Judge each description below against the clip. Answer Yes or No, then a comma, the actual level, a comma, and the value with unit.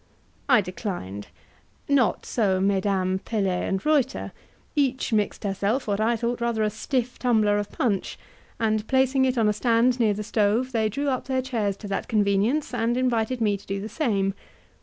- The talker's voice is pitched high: Yes, high, 220 Hz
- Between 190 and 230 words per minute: No, average, 180 wpm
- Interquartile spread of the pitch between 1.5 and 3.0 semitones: No, average, 3.9 semitones